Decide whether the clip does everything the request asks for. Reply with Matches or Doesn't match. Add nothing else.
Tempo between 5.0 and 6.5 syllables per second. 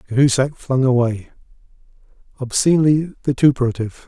Matches